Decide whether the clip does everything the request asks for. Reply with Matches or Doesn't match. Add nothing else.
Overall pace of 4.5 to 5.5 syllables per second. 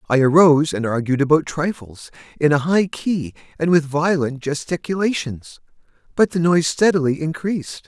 Matches